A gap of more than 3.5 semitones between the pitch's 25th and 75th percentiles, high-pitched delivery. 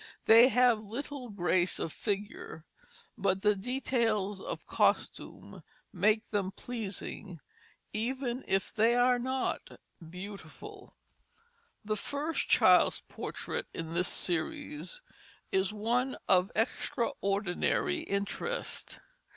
Yes: average, 4.5 semitones; high, 215 Hz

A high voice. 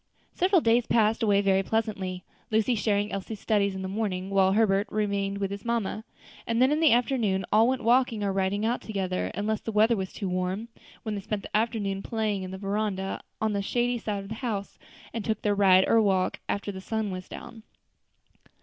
Yes: high, 205 Hz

